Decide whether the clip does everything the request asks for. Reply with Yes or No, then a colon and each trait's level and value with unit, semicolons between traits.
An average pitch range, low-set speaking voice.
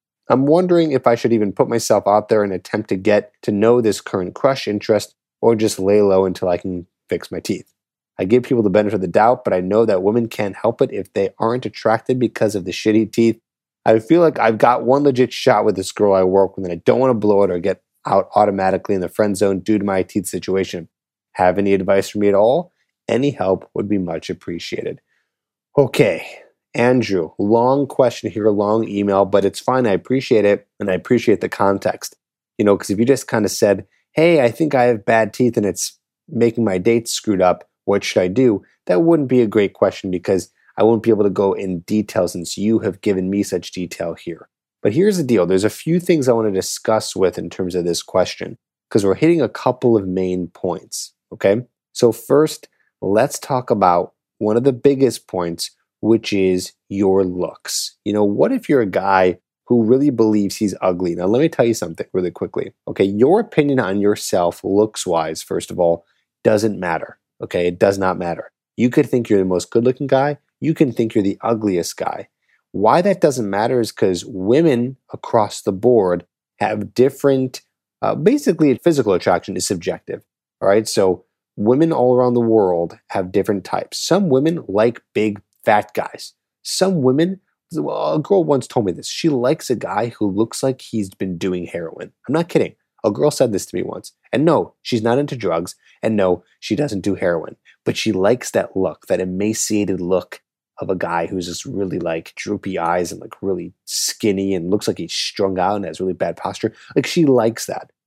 Yes: average, 4.5 semitones; low, 105 Hz